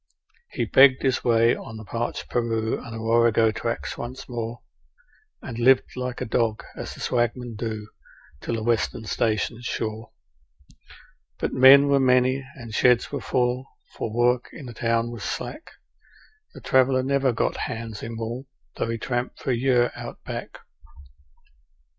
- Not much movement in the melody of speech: Yes, narrow, 1.9 semitones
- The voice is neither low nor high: No, low, 120 Hz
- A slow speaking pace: No, average, 160 wpm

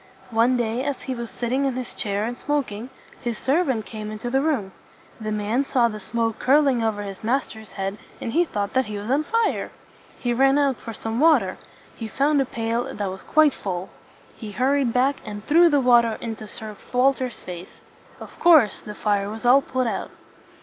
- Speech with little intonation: No, average, 4.0 semitones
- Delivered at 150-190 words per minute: No, average, 200 wpm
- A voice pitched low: No, high, 235 Hz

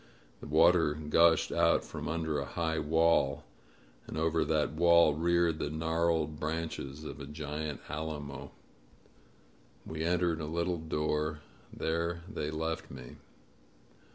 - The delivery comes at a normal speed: No, slow, 125 wpm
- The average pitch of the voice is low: Yes, very low, 80 Hz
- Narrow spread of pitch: Yes, narrow, 1.7 semitones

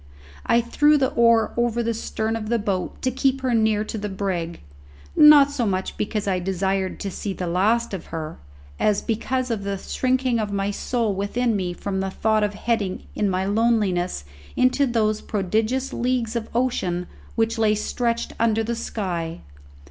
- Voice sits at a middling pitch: No, high, 215 Hz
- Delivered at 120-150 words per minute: No, average, 180 wpm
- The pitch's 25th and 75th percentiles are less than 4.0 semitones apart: Yes, average, 3.4 semitones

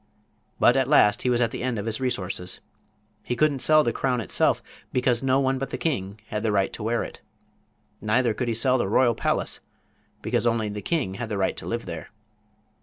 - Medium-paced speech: No, fast, 215 wpm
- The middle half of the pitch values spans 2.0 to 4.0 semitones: Yes, average, 3.5 semitones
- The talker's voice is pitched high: No, low, 120 Hz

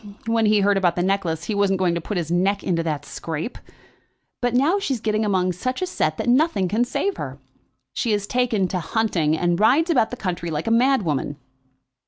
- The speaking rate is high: Yes, fast, 210 wpm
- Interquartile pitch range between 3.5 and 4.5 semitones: No, wide, 5.5 semitones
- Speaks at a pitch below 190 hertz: No, high, 200 Hz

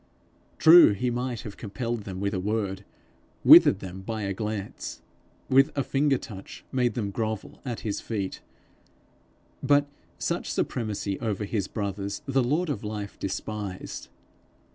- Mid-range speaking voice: No, low, 110 Hz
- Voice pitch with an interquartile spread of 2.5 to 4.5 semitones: Yes, average, 3.7 semitones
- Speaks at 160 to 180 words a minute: No, average, 140 wpm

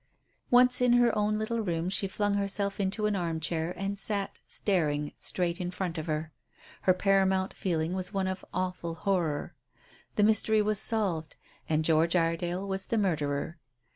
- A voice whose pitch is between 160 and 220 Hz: Yes, high, 190 Hz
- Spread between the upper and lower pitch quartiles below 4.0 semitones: Yes, average, 3.6 semitones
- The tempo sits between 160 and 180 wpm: Yes, average, 170 wpm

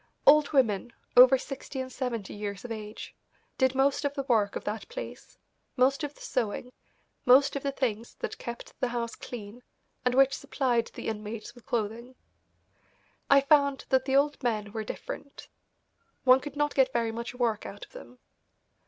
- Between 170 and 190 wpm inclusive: Yes, average, 175 wpm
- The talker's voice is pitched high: Yes, very high, 250 Hz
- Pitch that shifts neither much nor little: Yes, average, 3.3 semitones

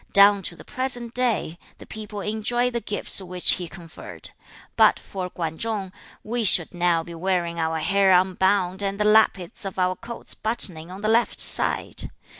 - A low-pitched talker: No, high, 195 Hz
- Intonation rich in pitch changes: No, average, 3.5 semitones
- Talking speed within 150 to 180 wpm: Yes, average, 175 wpm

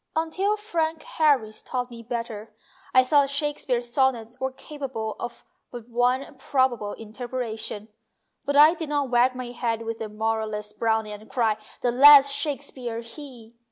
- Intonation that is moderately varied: Yes, average, 4.0 semitones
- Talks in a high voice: Yes, high, 245 Hz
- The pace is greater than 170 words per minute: No, average, 150 wpm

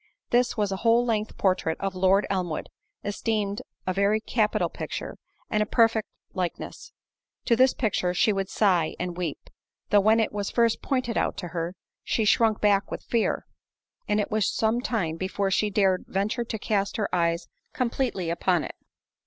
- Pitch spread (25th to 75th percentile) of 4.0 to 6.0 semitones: No, average, 3.2 semitones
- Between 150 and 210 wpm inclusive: Yes, average, 170 wpm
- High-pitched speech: Yes, high, 205 Hz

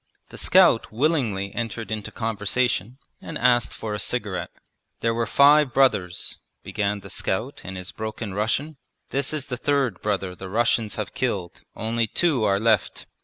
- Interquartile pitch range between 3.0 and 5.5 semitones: Yes, average, 4.0 semitones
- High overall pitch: No, low, 110 Hz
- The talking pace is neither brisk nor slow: Yes, average, 160 wpm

